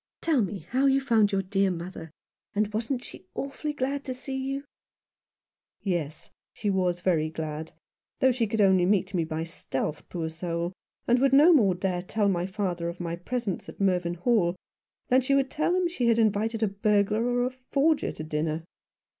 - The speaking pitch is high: Yes, high, 205 Hz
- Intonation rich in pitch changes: Yes, wide, 6.4 semitones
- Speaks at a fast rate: No, average, 195 wpm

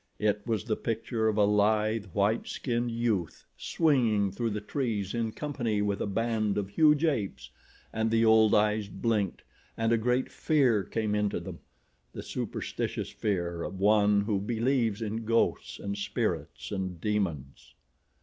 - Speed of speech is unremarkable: Yes, average, 150 wpm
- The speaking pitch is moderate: No, low, 110 Hz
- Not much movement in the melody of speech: Yes, narrow, 2.2 semitones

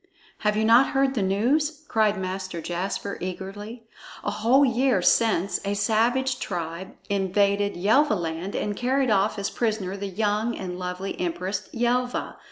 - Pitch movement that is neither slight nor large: Yes, average, 3.9 semitones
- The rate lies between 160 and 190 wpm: No, average, 145 wpm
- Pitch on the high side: Yes, high, 205 Hz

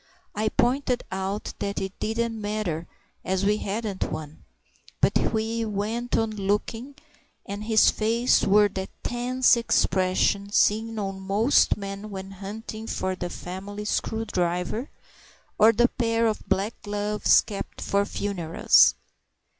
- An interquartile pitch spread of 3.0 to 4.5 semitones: No, narrow, 2.5 semitones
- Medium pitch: No, high, 210 Hz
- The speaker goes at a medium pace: No, slow, 130 wpm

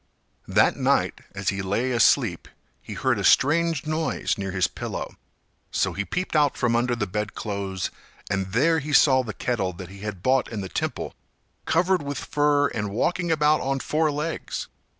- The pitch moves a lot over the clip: Yes, wide, 7.0 semitones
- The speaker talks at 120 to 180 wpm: Yes, average, 175 wpm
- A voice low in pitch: Yes, low, 125 Hz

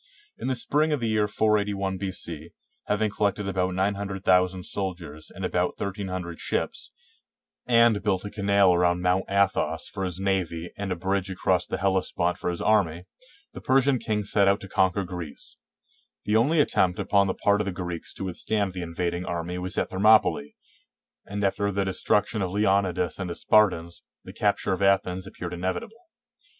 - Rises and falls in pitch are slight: Yes, narrow, 2.2 semitones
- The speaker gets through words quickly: No, average, 175 wpm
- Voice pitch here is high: No, very low, 95 Hz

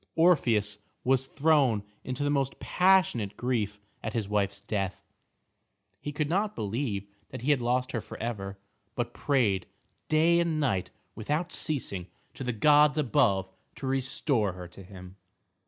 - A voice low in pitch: Yes, low, 125 Hz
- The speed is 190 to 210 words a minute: No, average, 145 wpm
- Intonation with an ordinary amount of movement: No, wide, 6.3 semitones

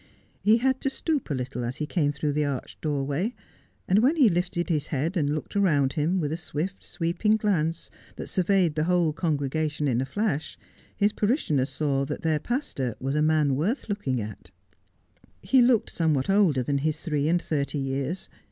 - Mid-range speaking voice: Yes, medium, 155 Hz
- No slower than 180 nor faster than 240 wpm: Yes, average, 190 wpm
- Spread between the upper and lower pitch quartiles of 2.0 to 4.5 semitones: No, average, 5.2 semitones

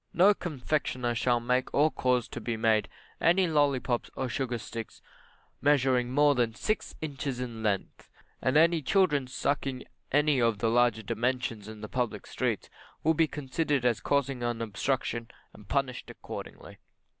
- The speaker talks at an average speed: Yes, average, 150 wpm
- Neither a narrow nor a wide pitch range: Yes, average, 3.7 semitones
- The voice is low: Yes, low, 125 Hz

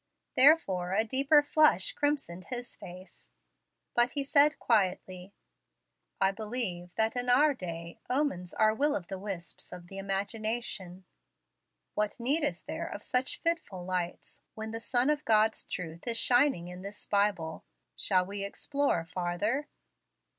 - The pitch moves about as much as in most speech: No, wide, 5.9 semitones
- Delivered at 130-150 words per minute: Yes, average, 145 wpm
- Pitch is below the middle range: No, high, 210 Hz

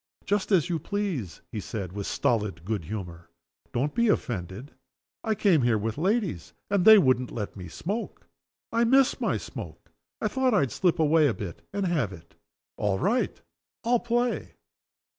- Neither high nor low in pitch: Yes, medium, 145 Hz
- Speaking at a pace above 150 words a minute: Yes, average, 165 wpm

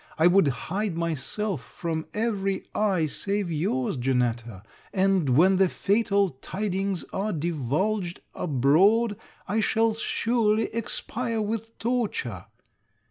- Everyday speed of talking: No, slow, 110 wpm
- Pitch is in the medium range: No, high, 195 Hz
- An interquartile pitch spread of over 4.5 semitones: Yes, average, 5.2 semitones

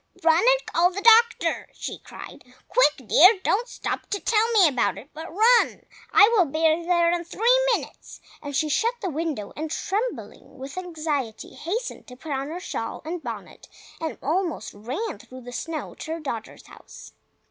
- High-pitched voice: Yes, very high, 330 Hz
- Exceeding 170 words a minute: Yes, average, 180 wpm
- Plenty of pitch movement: Yes, wide, 6.1 semitones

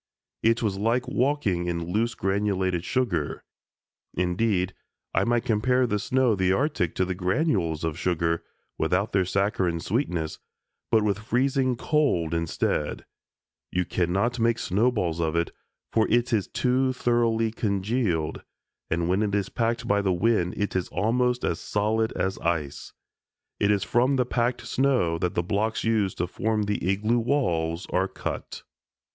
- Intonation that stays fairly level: No, average, 4.8 semitones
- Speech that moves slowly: No, average, 155 wpm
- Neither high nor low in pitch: No, low, 105 Hz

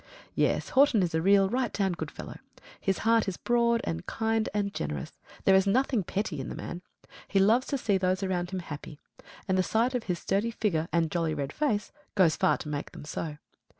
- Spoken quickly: Yes, fast, 215 wpm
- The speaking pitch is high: Yes, high, 195 Hz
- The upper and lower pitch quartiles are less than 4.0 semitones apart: No, average, 4.7 semitones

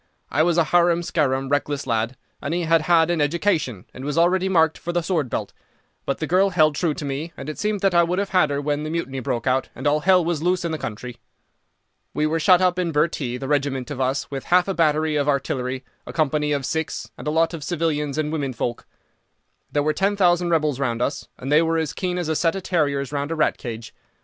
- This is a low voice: No, medium, 155 Hz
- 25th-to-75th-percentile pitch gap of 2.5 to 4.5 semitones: Yes, average, 3.6 semitones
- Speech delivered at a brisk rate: Yes, fast, 245 wpm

